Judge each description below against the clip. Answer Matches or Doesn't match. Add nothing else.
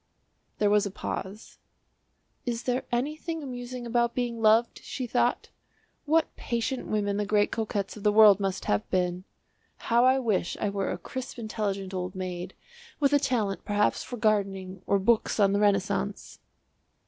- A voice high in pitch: Matches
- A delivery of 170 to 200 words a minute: Doesn't match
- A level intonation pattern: Doesn't match